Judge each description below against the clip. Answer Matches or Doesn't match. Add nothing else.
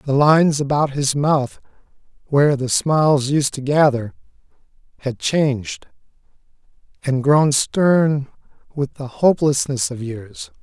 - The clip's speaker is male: Matches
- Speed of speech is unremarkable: Doesn't match